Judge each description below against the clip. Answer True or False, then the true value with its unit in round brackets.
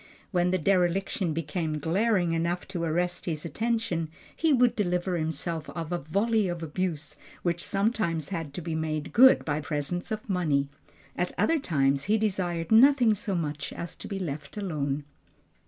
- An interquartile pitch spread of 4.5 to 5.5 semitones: False (4.0 semitones)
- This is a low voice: False (175 Hz)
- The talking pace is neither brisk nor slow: True (165 wpm)